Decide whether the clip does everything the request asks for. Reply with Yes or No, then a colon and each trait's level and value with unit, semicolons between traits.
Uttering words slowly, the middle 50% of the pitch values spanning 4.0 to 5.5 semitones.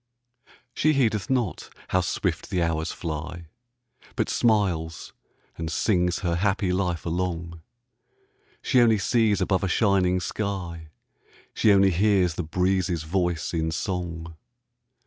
No: slow, 125 wpm; average, 3.1 semitones